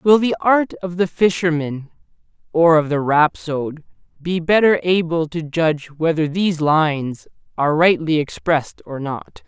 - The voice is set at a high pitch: No, medium, 165 Hz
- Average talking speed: Yes, average, 145 wpm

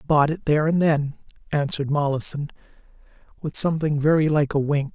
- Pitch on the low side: No, medium, 150 Hz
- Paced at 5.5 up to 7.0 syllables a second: Yes, 5.9 syllables/s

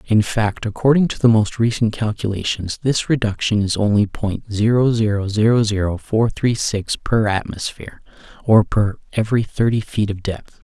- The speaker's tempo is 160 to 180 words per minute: Yes, average, 165 wpm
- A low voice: Yes, low, 110 Hz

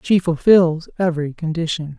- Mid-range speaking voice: Yes, medium, 165 Hz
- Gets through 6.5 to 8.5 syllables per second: No, 5.0 syllables/s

